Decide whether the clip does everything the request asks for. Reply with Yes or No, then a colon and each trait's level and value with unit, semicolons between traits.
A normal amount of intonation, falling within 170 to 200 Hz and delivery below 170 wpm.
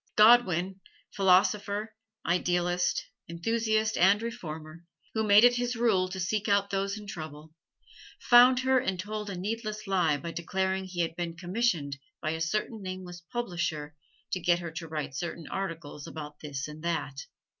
Yes: average, 4.3 semitones; medium, 185 Hz; average, 155 wpm